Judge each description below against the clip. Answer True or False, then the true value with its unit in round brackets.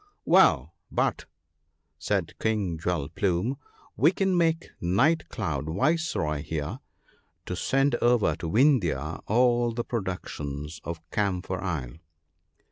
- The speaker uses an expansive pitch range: True (7.7 semitones)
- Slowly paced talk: True (115 wpm)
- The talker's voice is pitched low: True (95 Hz)